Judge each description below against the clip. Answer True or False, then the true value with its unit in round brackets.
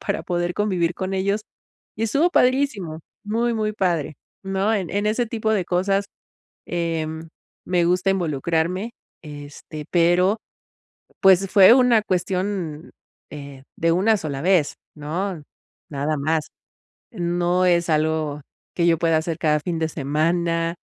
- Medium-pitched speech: True (175 Hz)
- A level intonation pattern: False (3.7 semitones)